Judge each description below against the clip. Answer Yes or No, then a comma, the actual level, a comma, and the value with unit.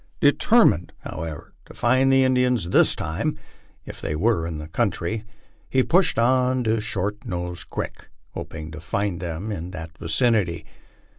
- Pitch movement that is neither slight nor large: No, wide, 6.7 semitones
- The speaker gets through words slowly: No, average, 150 wpm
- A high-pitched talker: No, low, 100 Hz